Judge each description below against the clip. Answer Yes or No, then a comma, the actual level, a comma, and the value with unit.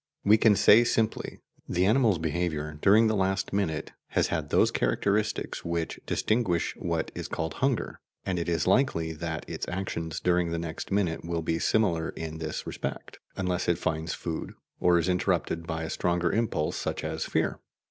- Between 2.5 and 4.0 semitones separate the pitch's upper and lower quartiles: Yes, average, 3.5 semitones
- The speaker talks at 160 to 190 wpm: Yes, average, 175 wpm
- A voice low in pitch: Yes, very low, 85 Hz